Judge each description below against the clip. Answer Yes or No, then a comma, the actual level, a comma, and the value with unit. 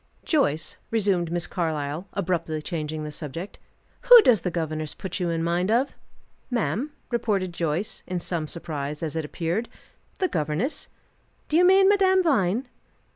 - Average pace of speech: Yes, average, 150 wpm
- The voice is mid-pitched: Yes, medium, 175 Hz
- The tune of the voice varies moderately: No, wide, 6.5 semitones